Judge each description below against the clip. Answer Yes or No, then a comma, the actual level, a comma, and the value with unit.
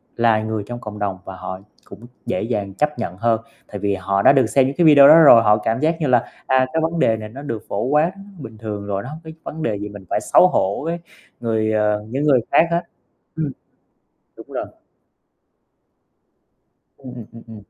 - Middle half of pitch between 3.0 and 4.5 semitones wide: No, average, 5.2 semitones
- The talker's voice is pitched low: Yes, low, 115 Hz